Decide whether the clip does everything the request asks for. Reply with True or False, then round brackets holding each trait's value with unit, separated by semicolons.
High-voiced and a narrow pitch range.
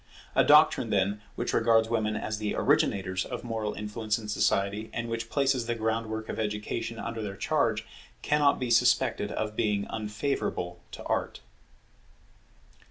False (110 Hz; 1.7 semitones)